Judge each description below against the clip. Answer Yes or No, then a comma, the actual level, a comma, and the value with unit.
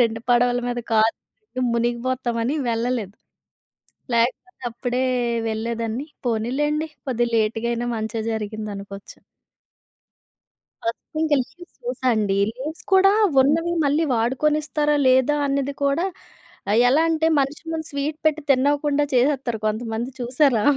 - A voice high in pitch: Yes, very high, 250 Hz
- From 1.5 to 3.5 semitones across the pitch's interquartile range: No, average, 4.4 semitones